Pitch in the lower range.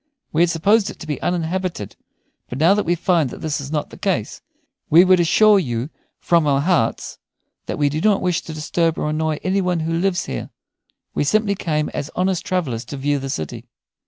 No: medium, 165 Hz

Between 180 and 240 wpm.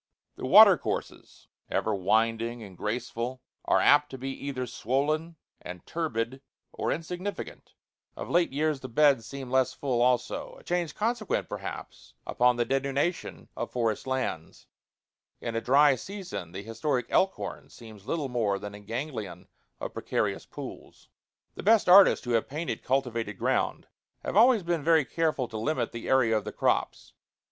No: average, 155 wpm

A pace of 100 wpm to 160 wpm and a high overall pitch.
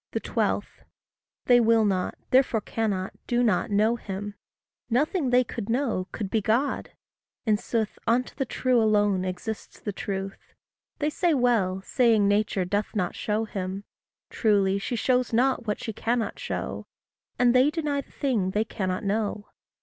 Yes: average, 155 wpm; high, 220 Hz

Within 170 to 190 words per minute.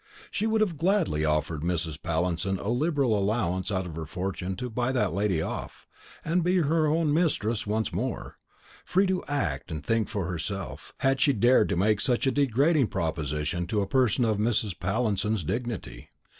Yes: average, 180 wpm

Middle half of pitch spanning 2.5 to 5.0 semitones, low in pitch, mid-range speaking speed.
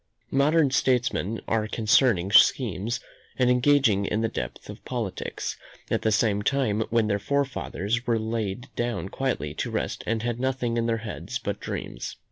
Yes: average, 3.3 semitones; low, 115 Hz; average, 155 wpm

